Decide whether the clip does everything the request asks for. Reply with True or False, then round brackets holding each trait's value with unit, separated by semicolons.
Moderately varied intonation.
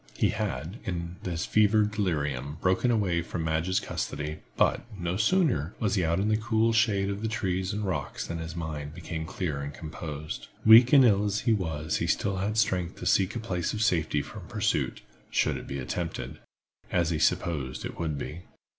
True (5.0 semitones)